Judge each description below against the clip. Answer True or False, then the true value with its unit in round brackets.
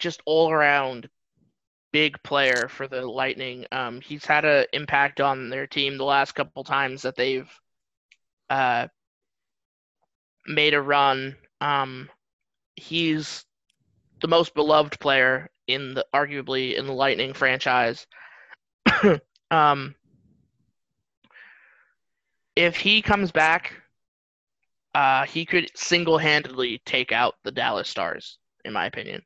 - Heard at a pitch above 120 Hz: True (140 Hz)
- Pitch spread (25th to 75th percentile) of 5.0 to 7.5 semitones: False (2.5 semitones)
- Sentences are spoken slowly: True (115 wpm)